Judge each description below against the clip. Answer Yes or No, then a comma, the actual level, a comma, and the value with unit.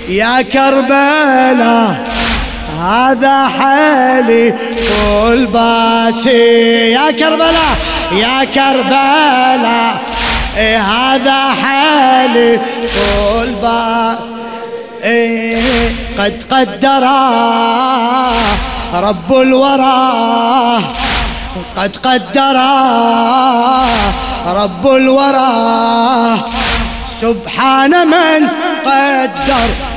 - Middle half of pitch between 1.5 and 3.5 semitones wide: Yes, narrow, 2.6 semitones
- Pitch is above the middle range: Yes, very high, 250 Hz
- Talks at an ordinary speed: No, slow, 45 wpm